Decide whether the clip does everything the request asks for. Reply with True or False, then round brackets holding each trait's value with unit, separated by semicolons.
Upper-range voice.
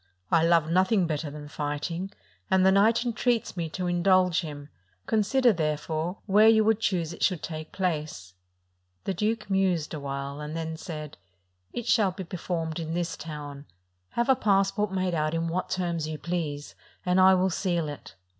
False (175 Hz)